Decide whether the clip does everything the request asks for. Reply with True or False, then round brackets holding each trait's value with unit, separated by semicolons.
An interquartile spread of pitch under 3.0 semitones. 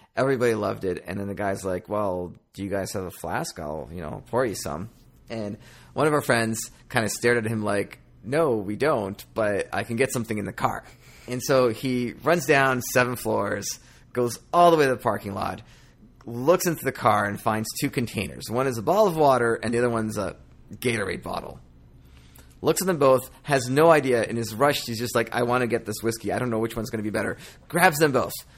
False (4.0 semitones)